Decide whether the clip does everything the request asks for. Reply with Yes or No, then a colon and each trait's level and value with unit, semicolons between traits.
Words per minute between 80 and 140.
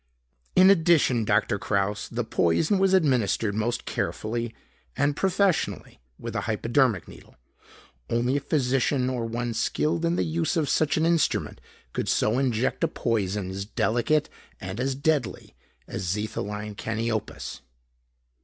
Yes: slow, 135 wpm